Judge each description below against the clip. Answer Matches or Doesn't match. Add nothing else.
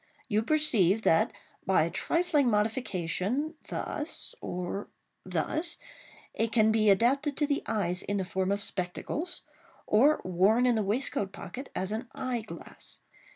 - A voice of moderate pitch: Doesn't match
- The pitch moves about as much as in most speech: Doesn't match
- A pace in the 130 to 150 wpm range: Matches